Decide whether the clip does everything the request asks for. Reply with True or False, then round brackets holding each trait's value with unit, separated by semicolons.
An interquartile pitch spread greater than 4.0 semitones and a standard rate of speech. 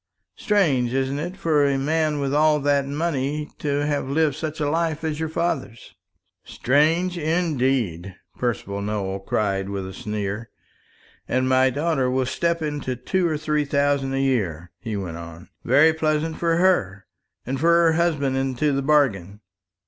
True (4.5 semitones; 160 wpm)